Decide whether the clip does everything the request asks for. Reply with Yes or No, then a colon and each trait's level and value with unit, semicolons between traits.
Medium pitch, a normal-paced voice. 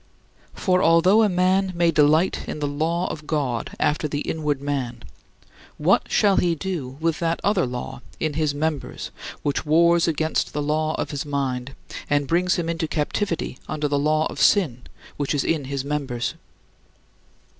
Yes: medium, 155 Hz; average, 165 wpm